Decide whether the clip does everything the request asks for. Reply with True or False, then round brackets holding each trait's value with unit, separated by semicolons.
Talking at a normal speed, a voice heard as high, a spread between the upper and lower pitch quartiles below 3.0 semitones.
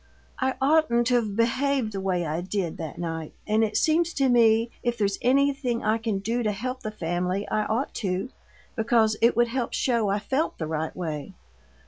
False (190 wpm; 220 Hz; 4.2 semitones)